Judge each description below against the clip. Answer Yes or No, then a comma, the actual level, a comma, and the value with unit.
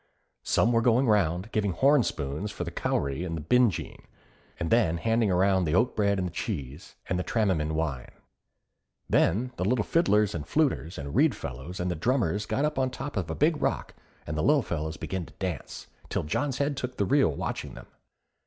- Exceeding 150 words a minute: Yes, average, 190 wpm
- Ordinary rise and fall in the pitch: No, wide, 7.1 semitones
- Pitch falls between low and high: No, very low, 95 Hz